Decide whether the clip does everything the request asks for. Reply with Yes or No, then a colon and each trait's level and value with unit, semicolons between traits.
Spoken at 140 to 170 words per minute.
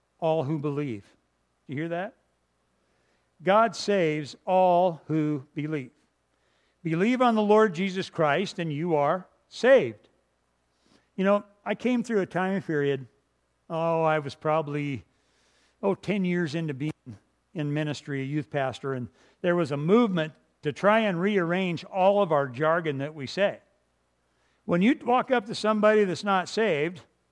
Yes: average, 150 wpm